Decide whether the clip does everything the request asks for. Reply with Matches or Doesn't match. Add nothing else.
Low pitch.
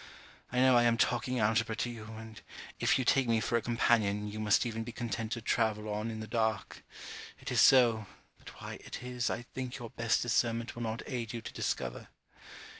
Matches